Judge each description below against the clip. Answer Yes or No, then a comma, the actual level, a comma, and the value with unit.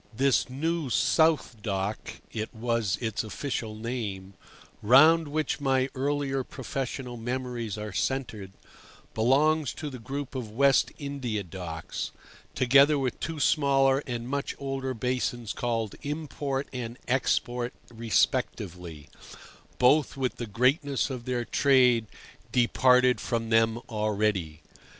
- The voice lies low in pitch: Yes, low, 125 Hz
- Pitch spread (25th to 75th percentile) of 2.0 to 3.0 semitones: No, average, 3.5 semitones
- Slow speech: Yes, slow, 120 wpm